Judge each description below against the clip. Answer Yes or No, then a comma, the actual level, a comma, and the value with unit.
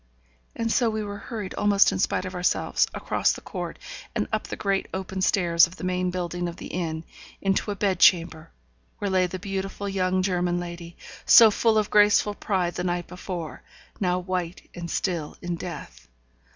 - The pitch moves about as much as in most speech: No, narrow, 2.2 semitones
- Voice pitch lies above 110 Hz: Yes, medium, 185 Hz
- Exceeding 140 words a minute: Yes, average, 185 wpm